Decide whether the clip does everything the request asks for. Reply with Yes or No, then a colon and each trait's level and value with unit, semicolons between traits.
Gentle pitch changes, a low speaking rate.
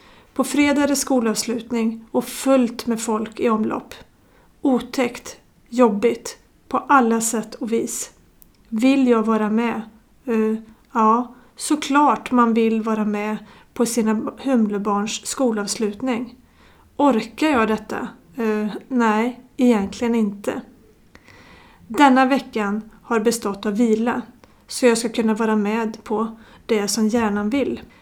Yes: narrow, 2.2 semitones; slow, 120 wpm